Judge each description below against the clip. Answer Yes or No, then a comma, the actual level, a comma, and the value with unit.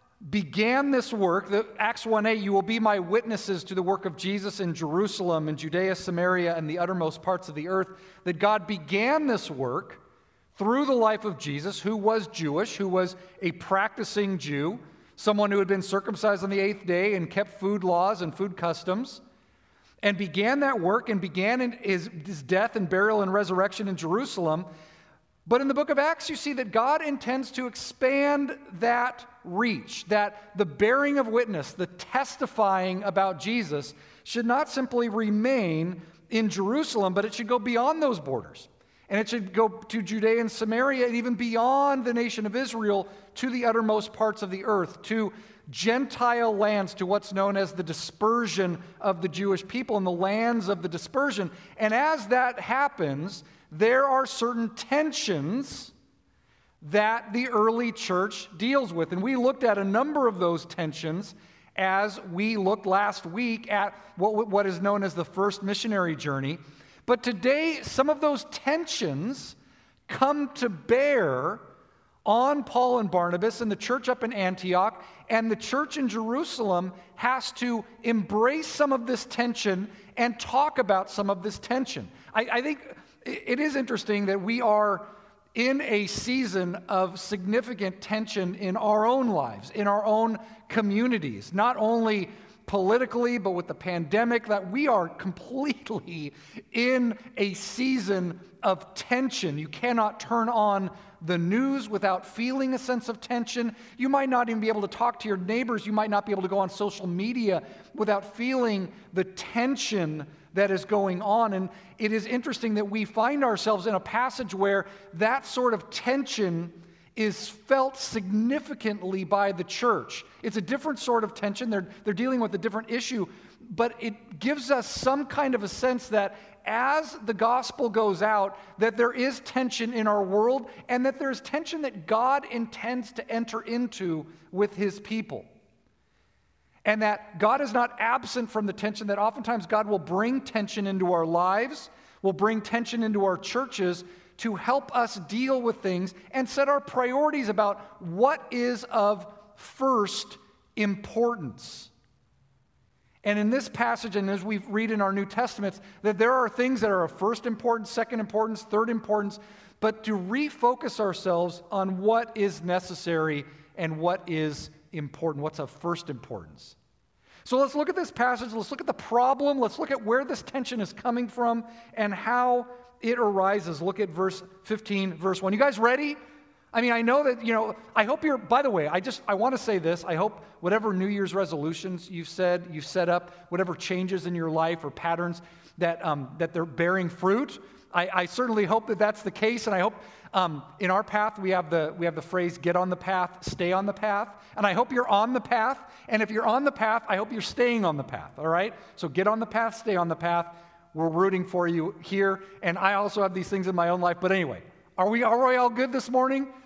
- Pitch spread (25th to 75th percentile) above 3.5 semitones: Yes, average, 4.2 semitones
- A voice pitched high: Yes, high, 210 Hz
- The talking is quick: No, average, 180 wpm